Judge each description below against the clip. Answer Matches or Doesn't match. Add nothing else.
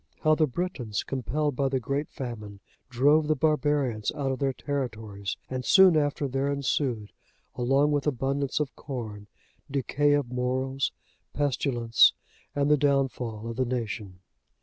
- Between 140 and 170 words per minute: Matches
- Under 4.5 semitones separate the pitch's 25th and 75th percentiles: Matches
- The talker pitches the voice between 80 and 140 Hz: Matches